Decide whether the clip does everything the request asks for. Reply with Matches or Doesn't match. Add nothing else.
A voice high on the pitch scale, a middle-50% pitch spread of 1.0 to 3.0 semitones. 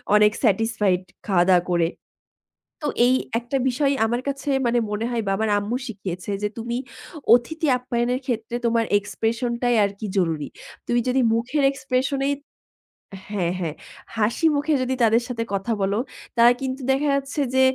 Doesn't match